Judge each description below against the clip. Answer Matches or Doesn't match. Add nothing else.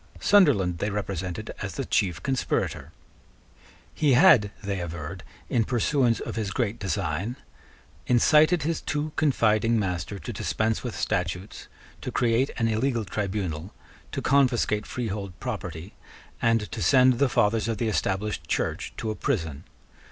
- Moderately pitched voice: Doesn't match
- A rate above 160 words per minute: Doesn't match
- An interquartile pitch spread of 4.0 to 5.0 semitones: Matches